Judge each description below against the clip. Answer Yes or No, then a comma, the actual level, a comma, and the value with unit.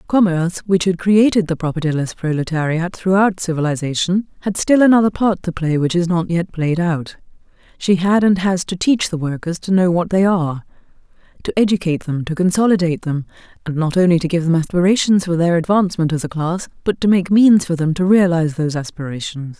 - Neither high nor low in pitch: Yes, medium, 175 Hz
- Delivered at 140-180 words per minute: No, average, 195 wpm